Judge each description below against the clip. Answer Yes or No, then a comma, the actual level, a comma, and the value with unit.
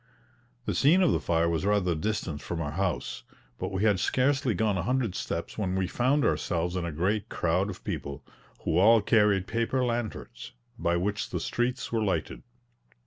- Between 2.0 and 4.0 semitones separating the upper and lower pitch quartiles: No, average, 5.1 semitones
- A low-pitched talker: Yes, low, 100 Hz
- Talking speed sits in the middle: Yes, average, 190 wpm